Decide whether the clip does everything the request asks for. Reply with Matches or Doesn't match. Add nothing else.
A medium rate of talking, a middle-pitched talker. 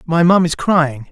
Doesn't match